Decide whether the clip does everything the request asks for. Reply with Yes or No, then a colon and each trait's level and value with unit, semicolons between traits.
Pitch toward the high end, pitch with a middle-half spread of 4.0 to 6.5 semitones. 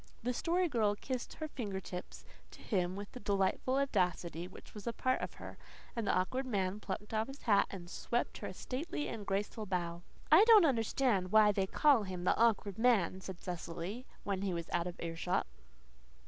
Yes: high, 205 Hz; average, 5.2 semitones